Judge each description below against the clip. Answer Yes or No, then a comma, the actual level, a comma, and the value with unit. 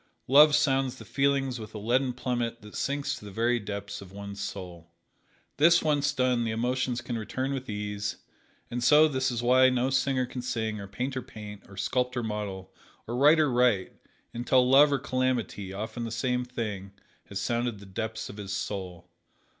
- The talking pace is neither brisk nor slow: Yes, average, 180 wpm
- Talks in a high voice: No, low, 120 Hz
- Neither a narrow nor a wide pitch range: Yes, average, 4.0 semitones